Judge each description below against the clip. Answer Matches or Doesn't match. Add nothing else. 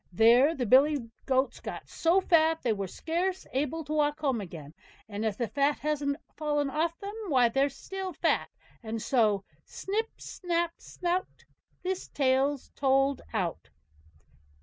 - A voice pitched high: Matches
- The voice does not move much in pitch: Doesn't match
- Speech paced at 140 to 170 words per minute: Matches